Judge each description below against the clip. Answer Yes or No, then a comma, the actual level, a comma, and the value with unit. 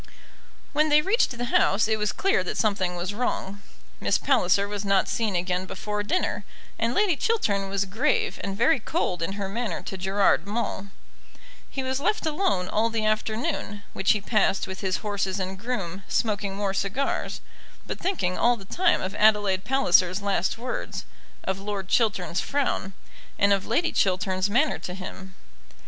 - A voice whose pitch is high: Yes, high, 205 Hz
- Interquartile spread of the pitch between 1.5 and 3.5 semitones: No, average, 3.9 semitones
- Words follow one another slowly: No, average, 170 wpm